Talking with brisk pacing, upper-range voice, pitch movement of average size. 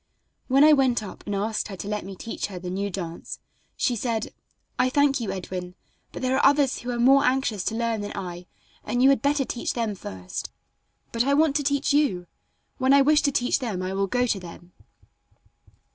No: fast, 215 wpm; high, 235 Hz; wide, 5.7 semitones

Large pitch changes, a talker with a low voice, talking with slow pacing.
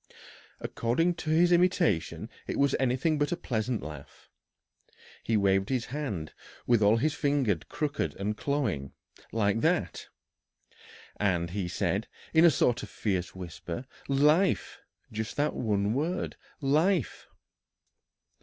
Yes: wide, 7.0 semitones; low, 120 Hz; slow, 125 wpm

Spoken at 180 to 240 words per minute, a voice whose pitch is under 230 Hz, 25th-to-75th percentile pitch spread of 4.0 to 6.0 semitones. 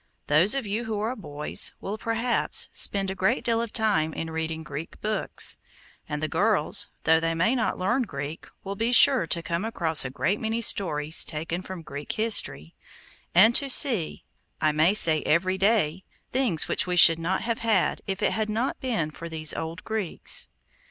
Yes: average, 185 wpm; medium, 185 Hz; wide, 5.5 semitones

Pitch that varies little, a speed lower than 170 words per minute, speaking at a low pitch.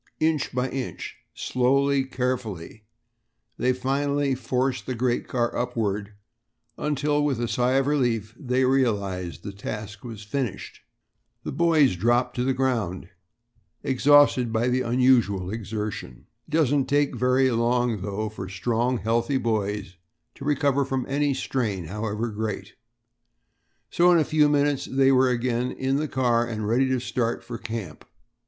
No: average, 3.6 semitones; average, 145 wpm; low, 125 Hz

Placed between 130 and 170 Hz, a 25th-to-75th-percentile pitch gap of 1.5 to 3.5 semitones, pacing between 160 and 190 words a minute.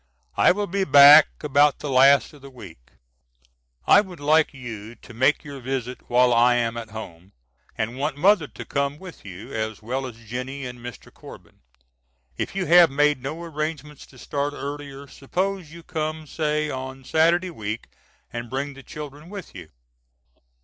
No: medium, 140 Hz; average, 3.9 semitones; average, 170 wpm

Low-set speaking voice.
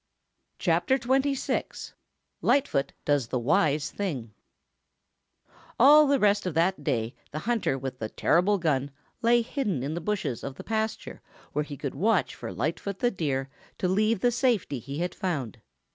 No: medium, 175 Hz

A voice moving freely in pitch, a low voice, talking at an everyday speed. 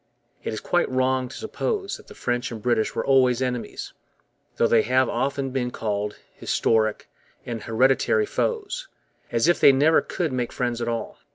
No: average, 2.9 semitones; low, 125 Hz; average, 175 wpm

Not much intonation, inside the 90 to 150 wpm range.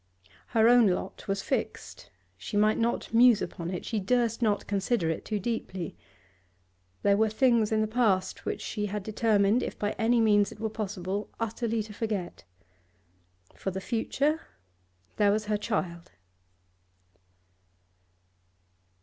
Yes: narrow, 2.3 semitones; average, 140 wpm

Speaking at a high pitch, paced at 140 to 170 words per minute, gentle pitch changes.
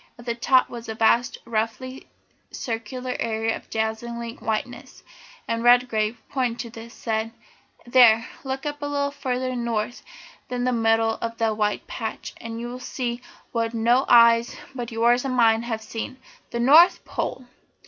Yes: high, 235 Hz; average, 160 wpm; narrow, 1.9 semitones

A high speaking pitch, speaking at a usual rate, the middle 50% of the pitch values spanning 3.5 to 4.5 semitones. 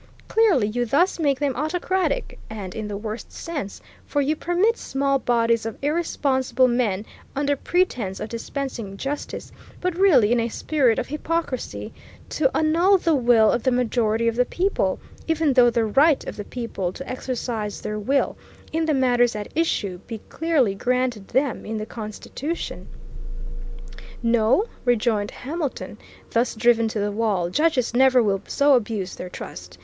No: high, 245 Hz; average, 160 wpm; average, 5.0 semitones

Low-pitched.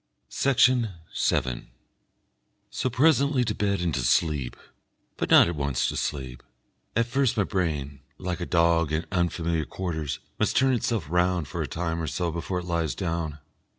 Yes: very low, 85 Hz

